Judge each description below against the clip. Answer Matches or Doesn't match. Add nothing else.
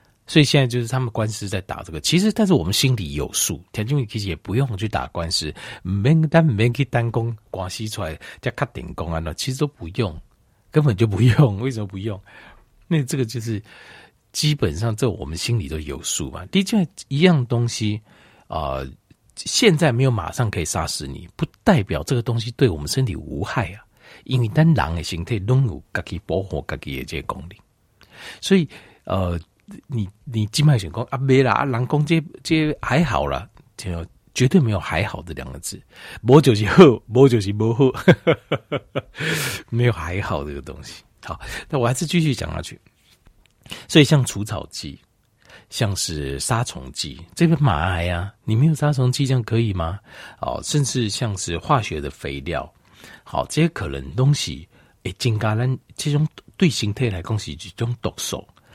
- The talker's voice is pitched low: Matches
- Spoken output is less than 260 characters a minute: Doesn't match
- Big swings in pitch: Matches